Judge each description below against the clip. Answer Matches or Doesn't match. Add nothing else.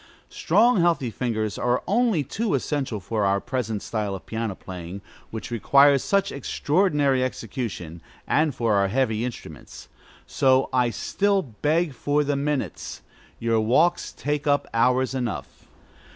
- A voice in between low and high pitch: Doesn't match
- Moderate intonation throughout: Matches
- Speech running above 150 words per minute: Doesn't match